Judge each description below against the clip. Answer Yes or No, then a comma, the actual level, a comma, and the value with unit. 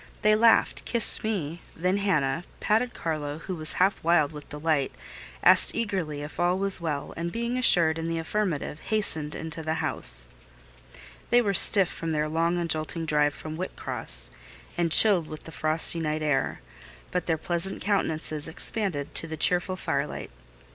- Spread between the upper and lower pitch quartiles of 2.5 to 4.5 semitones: Yes, average, 3.6 semitones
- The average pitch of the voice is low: No, medium, 165 Hz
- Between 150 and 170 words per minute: Yes, average, 160 wpm